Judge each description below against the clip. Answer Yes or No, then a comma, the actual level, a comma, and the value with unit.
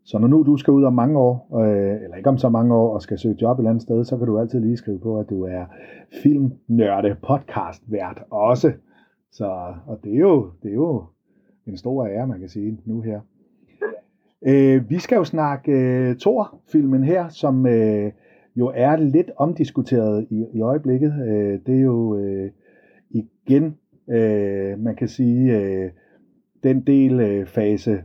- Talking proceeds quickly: No, average, 185 wpm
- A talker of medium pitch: No, low, 120 Hz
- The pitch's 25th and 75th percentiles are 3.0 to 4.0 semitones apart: No, average, 4.5 semitones